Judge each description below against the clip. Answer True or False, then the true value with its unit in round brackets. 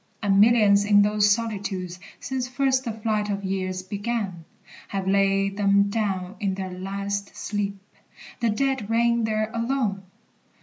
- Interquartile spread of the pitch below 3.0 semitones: True (2.4 semitones)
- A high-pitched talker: True (205 Hz)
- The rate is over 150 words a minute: False (140 wpm)